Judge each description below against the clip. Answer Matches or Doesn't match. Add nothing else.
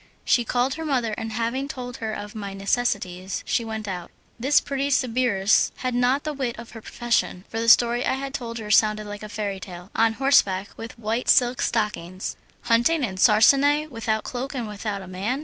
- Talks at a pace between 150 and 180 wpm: Doesn't match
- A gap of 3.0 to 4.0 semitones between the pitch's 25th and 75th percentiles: Matches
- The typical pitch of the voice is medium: Doesn't match